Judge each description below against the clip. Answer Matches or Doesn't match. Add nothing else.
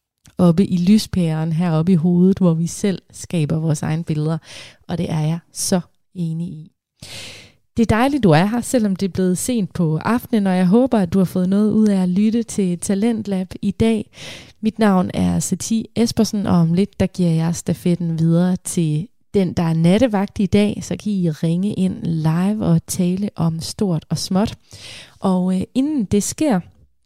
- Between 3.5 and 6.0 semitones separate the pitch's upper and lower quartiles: Matches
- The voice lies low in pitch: Doesn't match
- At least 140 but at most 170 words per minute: Doesn't match